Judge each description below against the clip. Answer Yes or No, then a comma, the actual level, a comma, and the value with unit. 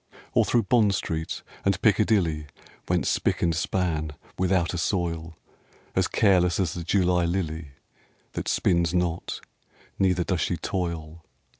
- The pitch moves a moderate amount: No, narrow, 2.2 semitones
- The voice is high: No, very low, 85 Hz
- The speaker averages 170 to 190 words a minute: No, slow, 135 wpm